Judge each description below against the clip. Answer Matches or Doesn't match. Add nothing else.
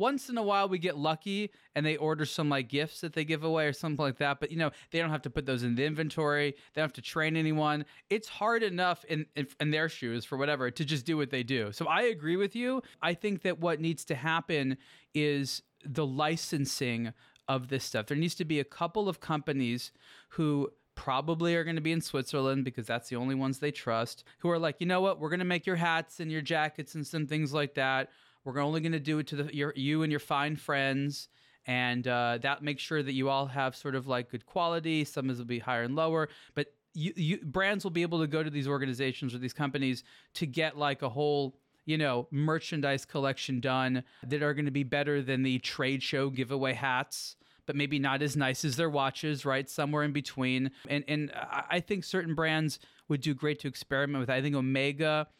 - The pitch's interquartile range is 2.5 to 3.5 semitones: Matches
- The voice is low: Doesn't match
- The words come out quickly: Matches